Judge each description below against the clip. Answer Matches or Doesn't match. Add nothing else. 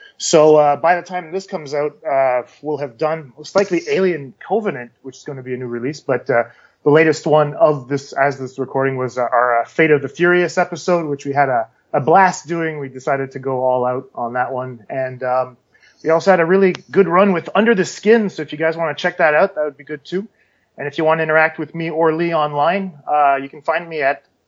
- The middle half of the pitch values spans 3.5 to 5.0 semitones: Matches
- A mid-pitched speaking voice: Matches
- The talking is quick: Matches